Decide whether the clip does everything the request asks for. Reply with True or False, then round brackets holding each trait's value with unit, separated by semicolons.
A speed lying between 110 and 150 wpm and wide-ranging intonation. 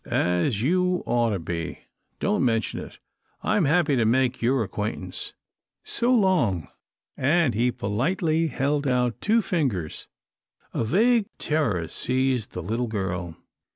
True (140 wpm; 7.5 semitones)